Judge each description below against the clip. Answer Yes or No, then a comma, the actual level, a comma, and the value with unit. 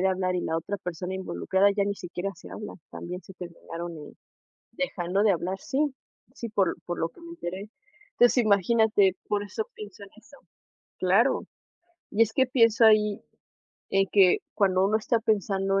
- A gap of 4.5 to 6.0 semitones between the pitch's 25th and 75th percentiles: No, average, 2.8 semitones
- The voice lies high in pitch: Yes, high, 195 Hz